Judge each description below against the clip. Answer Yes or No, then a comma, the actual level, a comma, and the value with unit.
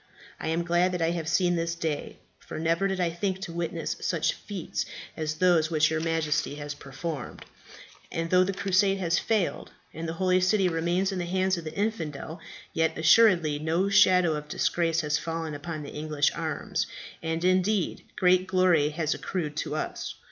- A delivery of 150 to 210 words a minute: Yes, average, 185 wpm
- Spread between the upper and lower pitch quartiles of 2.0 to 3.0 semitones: Yes, narrow, 2.6 semitones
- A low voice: No, medium, 170 Hz